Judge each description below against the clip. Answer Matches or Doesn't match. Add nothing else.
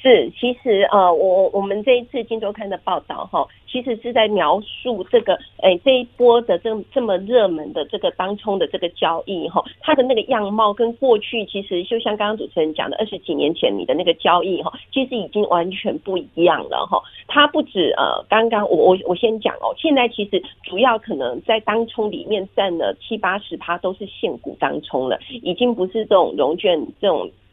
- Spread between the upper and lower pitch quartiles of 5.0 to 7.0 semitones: Doesn't match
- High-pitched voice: Matches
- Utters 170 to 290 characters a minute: Doesn't match